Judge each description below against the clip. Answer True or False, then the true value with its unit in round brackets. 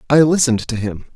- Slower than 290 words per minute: True (205 wpm)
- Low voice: True (125 Hz)